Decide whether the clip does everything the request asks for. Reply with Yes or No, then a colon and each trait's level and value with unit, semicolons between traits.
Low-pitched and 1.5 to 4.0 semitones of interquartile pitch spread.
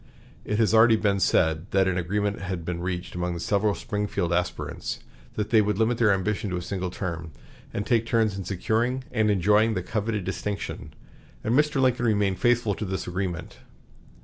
Yes: low, 100 Hz; average, 3.4 semitones